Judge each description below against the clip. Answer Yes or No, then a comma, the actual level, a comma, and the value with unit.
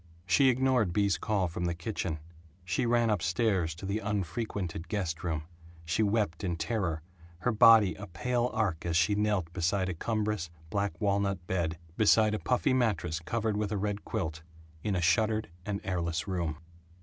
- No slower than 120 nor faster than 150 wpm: No, average, 175 wpm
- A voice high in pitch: No, low, 100 Hz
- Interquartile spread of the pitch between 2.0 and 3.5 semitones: No, average, 4.0 semitones